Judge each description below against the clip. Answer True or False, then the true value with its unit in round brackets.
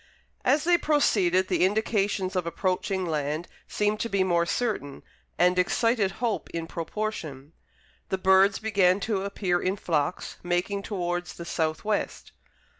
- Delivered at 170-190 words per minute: False (140 wpm)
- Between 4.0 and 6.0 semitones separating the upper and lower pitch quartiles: False (3.2 semitones)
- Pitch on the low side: False (190 Hz)